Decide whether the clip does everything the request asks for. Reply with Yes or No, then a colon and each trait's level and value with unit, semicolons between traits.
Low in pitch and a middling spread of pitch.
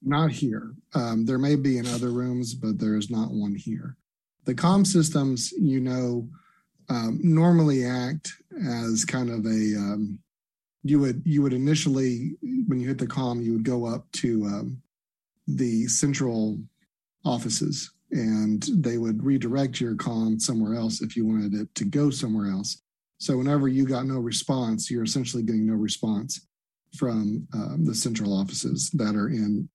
Yes: low, 125 Hz; average, 3.8 semitones